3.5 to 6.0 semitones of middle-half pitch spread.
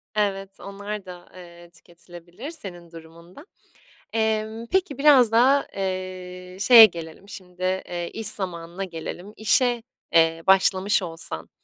Yes: average, 3.9 semitones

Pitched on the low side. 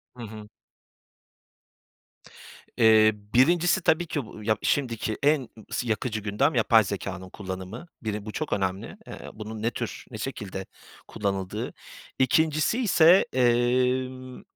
Yes: low, 115 Hz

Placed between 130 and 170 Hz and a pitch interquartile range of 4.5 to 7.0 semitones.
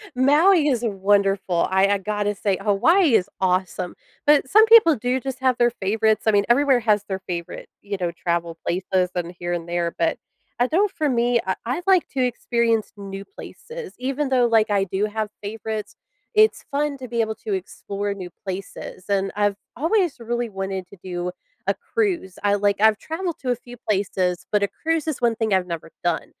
No: high, 215 Hz; wide, 5.4 semitones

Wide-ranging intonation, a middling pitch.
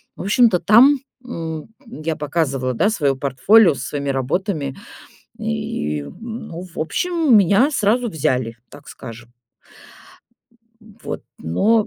Yes: wide, 8.3 semitones; medium, 165 Hz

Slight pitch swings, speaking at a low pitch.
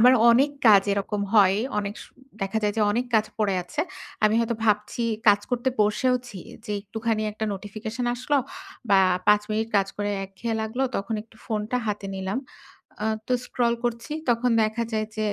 No: narrow, 2.3 semitones; high, 215 Hz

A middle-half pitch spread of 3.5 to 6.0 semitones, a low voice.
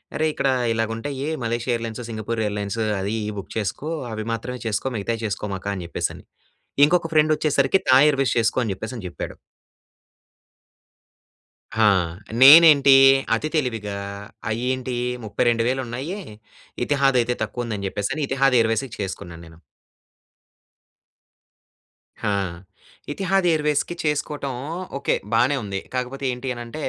Yes: average, 4.1 semitones; low, 125 Hz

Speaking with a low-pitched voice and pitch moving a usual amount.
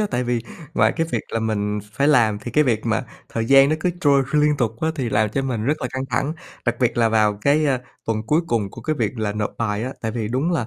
Yes: low, 120 Hz; average, 4.3 semitones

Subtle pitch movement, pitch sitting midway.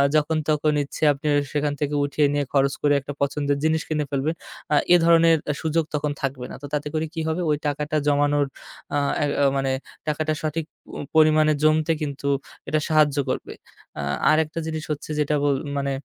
Yes: narrow, 1.5 semitones; medium, 150 Hz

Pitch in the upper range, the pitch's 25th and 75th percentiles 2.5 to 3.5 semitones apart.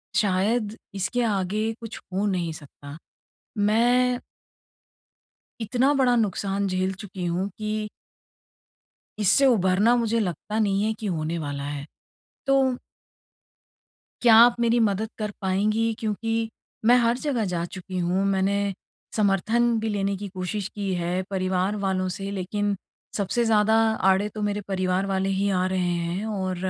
Yes: high, 200 Hz; average, 3.0 semitones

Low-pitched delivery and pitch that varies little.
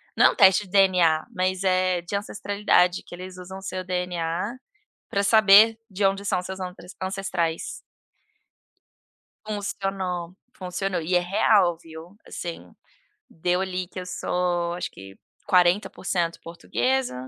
No: medium, 185 Hz; narrow, 2.0 semitones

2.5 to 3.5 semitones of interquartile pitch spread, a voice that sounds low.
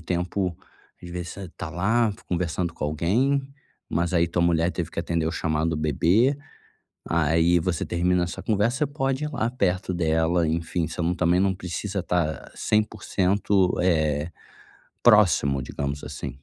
Yes: average, 3.2 semitones; very low, 90 Hz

